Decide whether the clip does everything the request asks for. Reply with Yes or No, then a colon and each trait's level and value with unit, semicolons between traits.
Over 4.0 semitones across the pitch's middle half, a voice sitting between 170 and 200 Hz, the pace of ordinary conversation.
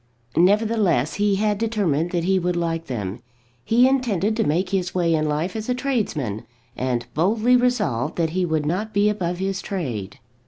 Yes: wide, 5.4 semitones; medium, 185 Hz; average, 180 wpm